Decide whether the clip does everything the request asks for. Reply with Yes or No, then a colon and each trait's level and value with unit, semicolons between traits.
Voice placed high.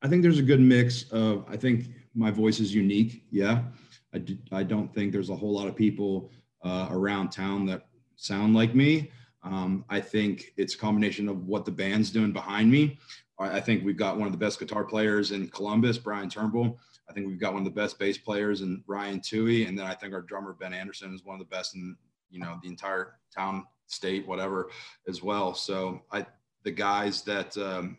No: low, 100 Hz